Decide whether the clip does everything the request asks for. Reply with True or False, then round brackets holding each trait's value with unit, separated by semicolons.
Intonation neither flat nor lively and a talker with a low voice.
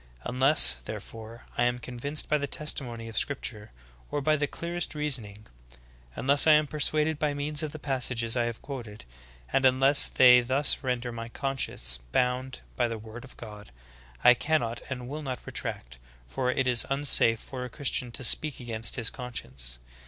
True (3.8 semitones; 125 Hz)